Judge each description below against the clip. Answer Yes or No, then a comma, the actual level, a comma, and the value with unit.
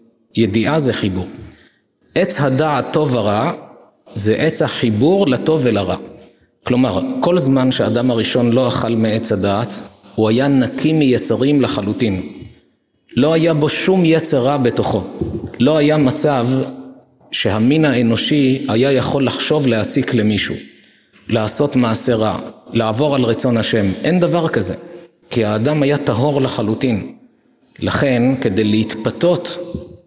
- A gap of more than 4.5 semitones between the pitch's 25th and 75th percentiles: Yes, average, 5.1 semitones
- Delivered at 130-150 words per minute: No, average, 120 wpm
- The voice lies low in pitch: Yes, low, 125 Hz